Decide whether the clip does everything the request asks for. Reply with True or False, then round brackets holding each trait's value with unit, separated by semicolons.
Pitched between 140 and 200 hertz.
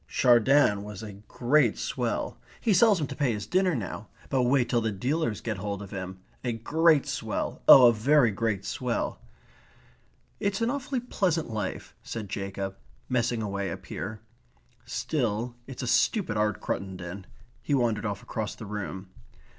False (115 Hz)